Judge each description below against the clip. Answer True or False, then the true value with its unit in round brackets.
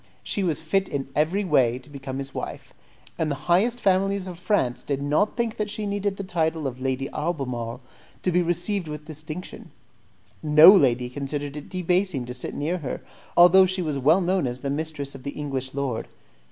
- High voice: False (155 Hz)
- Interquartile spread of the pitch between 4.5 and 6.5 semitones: True (5.1 semitones)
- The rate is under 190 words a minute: False (195 wpm)